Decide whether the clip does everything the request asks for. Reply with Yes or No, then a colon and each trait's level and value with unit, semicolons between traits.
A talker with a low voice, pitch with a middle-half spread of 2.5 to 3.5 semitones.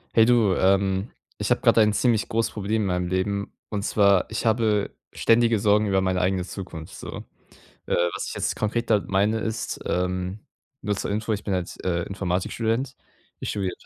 Yes: low, 100 Hz; average, 2.9 semitones